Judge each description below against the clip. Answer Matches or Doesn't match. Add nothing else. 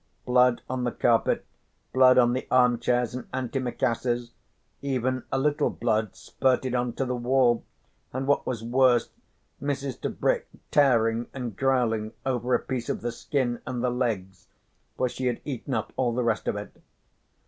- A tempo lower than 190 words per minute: Matches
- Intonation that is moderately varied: Doesn't match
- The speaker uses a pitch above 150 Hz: Doesn't match